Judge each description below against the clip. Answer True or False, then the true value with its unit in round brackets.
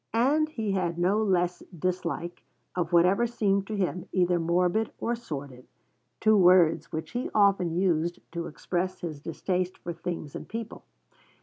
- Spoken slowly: False (150 wpm)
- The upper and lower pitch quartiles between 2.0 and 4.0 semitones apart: True (3.0 semitones)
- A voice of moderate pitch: True (180 Hz)